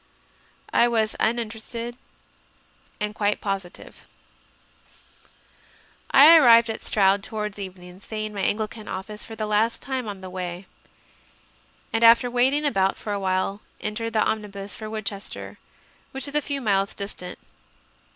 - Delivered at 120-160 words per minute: Yes, average, 140 wpm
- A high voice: Yes, high, 215 Hz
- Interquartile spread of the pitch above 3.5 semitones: No, average, 2.7 semitones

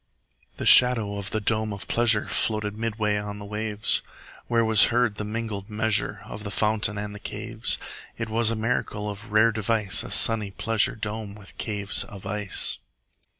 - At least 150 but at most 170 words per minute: No, average, 185 wpm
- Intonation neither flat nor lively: No, narrow, 1.4 semitones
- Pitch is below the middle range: Yes, low, 105 Hz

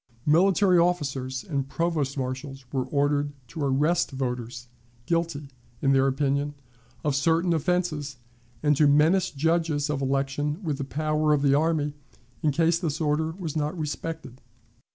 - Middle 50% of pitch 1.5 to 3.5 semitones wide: Yes, average, 3.0 semitones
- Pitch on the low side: No, medium, 150 Hz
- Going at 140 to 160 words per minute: Yes, average, 145 wpm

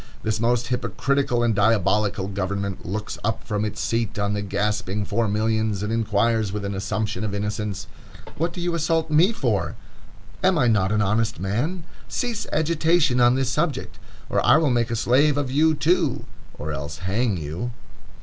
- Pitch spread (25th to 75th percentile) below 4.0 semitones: No, average, 5.3 semitones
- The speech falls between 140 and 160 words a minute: No, average, 175 wpm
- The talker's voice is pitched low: Yes, low, 110 Hz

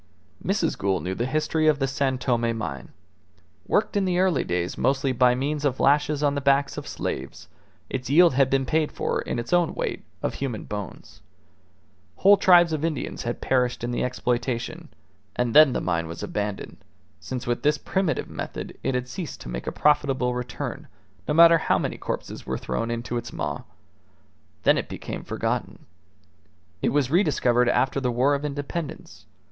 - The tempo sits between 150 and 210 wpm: Yes, average, 180 wpm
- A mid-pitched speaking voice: No, low, 130 Hz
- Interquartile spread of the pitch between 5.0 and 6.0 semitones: No, average, 4.0 semitones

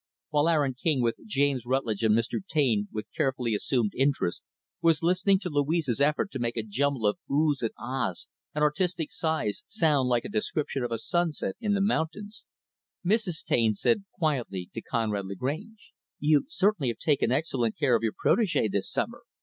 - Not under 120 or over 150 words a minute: No, average, 175 wpm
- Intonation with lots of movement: Yes, wide, 6.0 semitones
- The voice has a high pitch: No, medium, 140 Hz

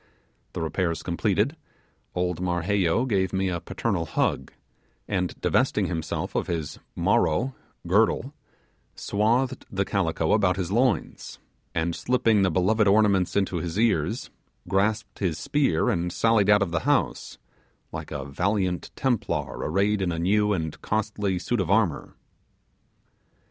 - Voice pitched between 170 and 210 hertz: No, very low, 95 Hz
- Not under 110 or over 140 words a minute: Yes, slow, 135 wpm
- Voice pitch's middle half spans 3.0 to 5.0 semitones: Yes, average, 3.6 semitones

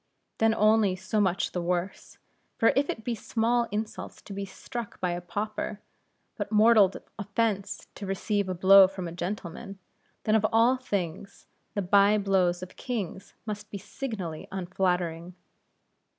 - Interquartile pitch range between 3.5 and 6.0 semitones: No, average, 3.0 semitones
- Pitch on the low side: No, high, 200 Hz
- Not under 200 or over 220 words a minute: No, average, 150 wpm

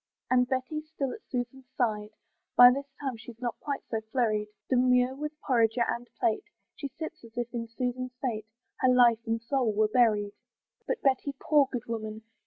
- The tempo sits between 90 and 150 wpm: No, average, 180 wpm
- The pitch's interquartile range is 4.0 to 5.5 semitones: No, average, 2.7 semitones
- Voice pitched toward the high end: Yes, high, 245 Hz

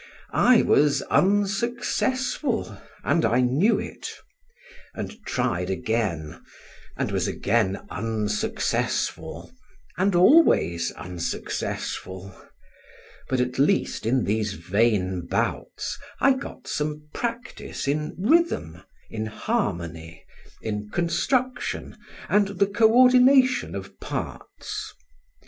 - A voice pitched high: No, medium, 140 Hz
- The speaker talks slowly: Yes, slow, 95 wpm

